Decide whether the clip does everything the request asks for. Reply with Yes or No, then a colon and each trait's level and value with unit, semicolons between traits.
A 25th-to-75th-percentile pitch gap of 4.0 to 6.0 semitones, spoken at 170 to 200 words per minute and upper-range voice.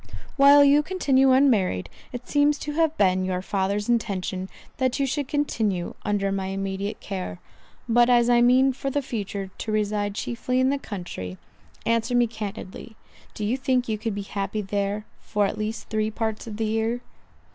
Yes: average, 4.4 semitones; average, 175 wpm; high, 220 Hz